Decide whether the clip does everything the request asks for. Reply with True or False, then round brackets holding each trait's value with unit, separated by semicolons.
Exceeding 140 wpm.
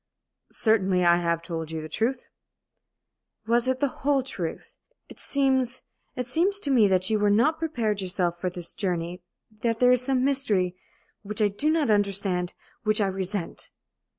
True (170 wpm)